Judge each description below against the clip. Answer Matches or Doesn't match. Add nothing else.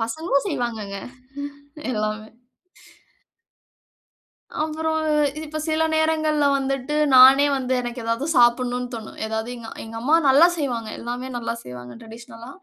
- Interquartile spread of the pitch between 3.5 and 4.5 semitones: Matches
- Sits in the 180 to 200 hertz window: Doesn't match